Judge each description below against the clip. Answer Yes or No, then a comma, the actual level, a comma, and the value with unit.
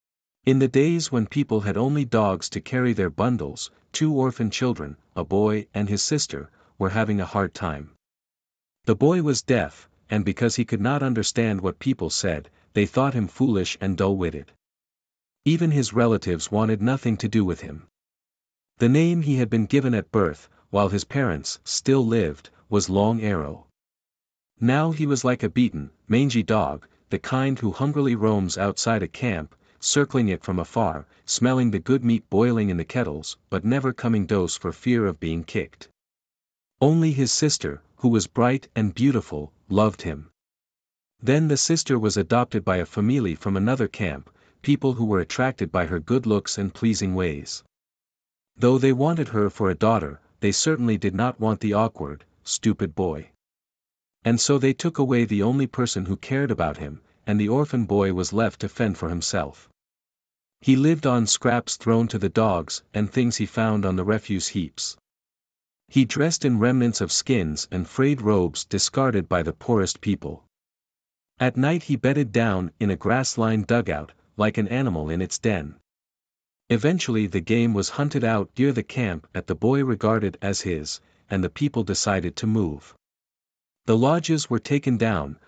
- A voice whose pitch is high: No, low, 110 Hz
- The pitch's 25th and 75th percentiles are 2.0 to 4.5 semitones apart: No, average, 5.3 semitones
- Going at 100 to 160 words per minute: No, average, 175 wpm